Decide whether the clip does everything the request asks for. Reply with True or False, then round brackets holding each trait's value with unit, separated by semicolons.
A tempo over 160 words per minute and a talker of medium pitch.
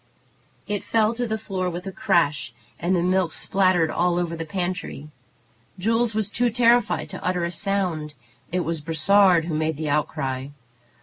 True (170 wpm; 180 Hz)